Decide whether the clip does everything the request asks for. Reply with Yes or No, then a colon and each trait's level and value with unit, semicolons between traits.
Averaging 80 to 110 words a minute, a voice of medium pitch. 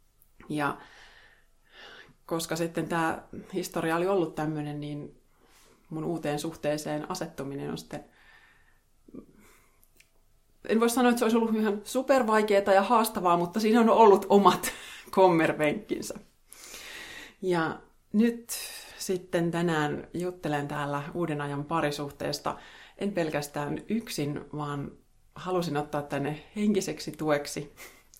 Yes: average, 105 wpm; medium, 170 Hz